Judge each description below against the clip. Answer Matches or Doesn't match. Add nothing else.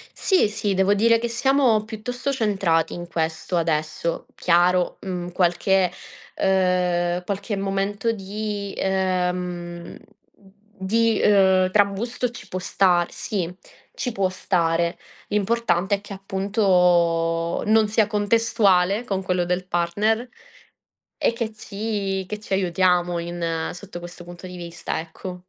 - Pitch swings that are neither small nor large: Matches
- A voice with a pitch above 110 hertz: Matches